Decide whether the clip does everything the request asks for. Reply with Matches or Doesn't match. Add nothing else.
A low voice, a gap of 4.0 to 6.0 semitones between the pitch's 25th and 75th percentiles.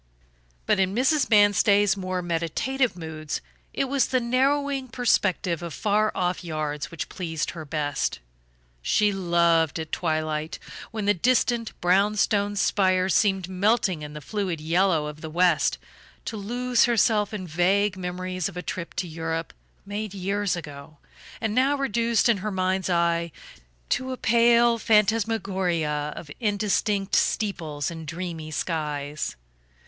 Doesn't match